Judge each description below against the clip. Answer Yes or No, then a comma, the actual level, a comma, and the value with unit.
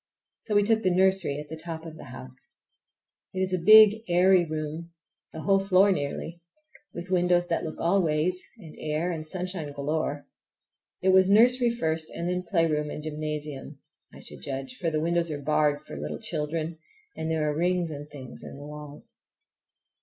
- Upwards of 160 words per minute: Yes, average, 185 wpm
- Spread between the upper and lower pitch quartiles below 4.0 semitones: Yes, average, 3.5 semitones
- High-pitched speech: No, medium, 160 Hz